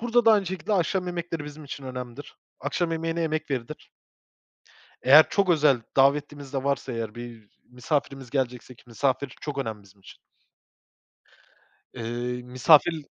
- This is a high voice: No, medium, 140 Hz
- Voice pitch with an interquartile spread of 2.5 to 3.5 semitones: No, average, 4.8 semitones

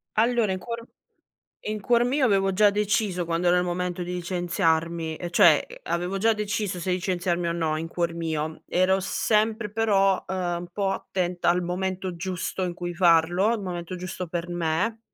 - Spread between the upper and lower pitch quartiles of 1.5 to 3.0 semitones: Yes, average, 2.7 semitones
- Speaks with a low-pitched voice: No, medium, 180 Hz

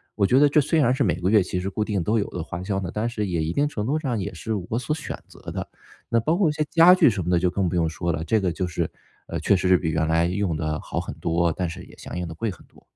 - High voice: No, very low, 95 Hz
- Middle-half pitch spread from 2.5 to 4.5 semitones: No, average, 5.1 semitones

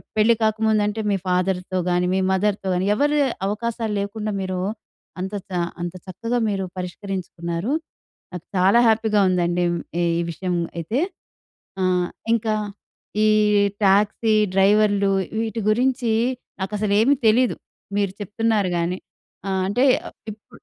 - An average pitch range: Yes, average, 3.1 semitones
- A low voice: No, high, 200 Hz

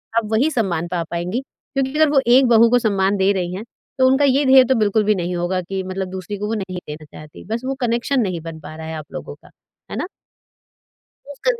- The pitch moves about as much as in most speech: No, wide, 6.0 semitones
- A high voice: Yes, high, 205 Hz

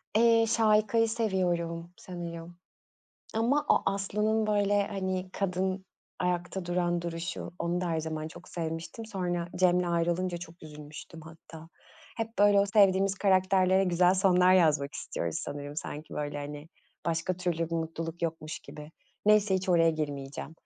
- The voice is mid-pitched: Yes, medium, 180 Hz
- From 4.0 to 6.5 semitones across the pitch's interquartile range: No, average, 3.0 semitones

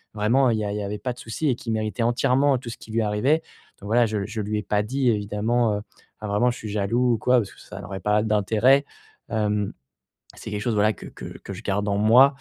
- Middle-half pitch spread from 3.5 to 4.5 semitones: No, average, 2.8 semitones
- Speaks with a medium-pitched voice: No, low, 110 Hz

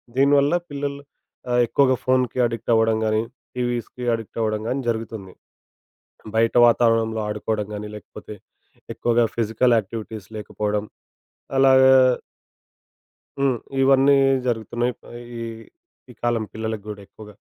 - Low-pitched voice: Yes, low, 115 Hz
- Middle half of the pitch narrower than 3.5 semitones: Yes, average, 2.9 semitones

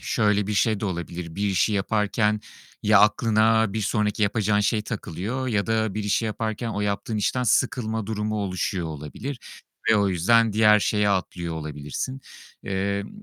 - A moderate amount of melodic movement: No, narrow, 2.1 semitones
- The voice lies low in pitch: Yes, low, 105 Hz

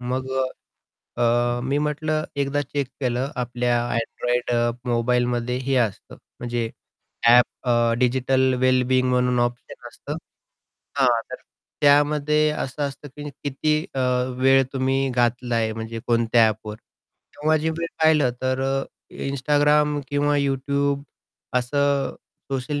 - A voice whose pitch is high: No, low, 130 Hz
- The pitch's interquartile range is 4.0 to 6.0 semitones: No, average, 2.8 semitones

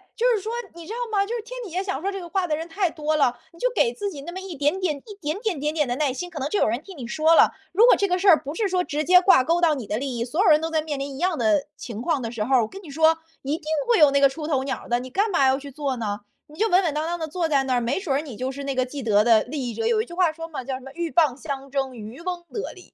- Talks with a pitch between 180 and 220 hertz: No, very high, 310 Hz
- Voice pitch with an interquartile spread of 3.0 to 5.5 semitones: Yes, average, 5.1 semitones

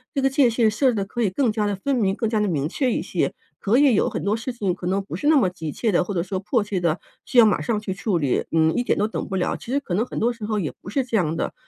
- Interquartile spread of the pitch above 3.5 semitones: Yes, average, 4.4 semitones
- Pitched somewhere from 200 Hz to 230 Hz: Yes, high, 210 Hz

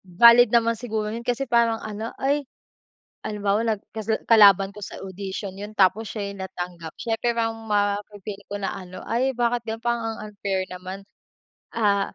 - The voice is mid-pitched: No, high, 210 Hz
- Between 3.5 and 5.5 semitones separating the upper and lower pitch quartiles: No, average, 2.8 semitones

